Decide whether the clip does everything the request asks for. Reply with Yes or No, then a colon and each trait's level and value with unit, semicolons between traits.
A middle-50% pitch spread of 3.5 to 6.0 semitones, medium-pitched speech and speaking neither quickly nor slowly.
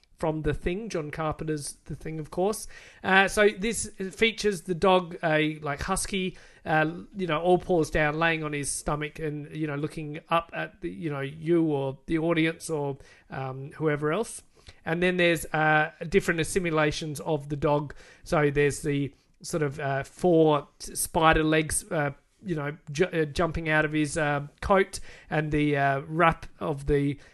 No: average, 2.7 semitones; medium, 155 Hz; average, 175 wpm